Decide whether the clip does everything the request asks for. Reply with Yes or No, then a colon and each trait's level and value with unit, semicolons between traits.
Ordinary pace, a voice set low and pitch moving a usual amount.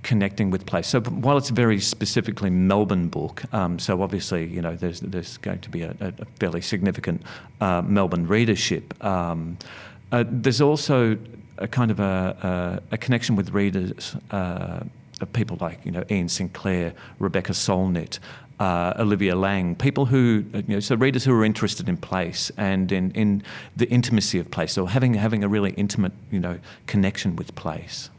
Yes: average, 175 wpm; low, 100 Hz; average, 3.5 semitones